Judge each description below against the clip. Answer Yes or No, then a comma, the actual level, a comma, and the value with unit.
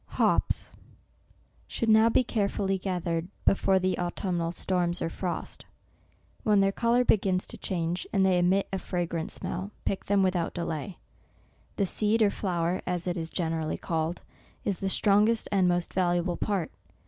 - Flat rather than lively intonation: Yes, narrow, 2.3 semitones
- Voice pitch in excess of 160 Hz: Yes, medium, 185 Hz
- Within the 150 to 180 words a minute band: Yes, average, 160 wpm